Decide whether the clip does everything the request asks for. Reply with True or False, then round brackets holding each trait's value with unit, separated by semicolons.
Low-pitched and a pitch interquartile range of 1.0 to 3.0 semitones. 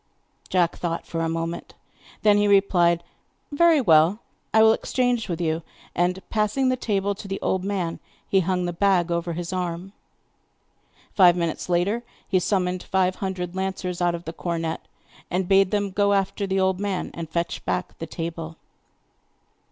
False (185 Hz; 2.7 semitones)